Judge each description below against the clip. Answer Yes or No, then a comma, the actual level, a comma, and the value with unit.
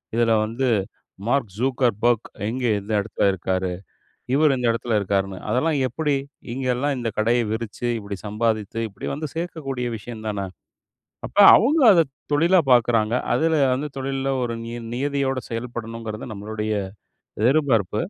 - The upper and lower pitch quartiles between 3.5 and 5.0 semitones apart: Yes, average, 3.9 semitones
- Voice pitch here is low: Yes, low, 120 Hz